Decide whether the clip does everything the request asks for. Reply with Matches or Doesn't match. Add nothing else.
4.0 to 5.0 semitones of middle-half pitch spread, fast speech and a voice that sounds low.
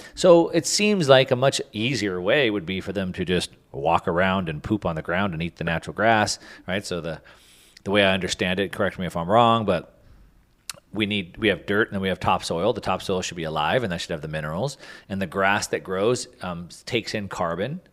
Matches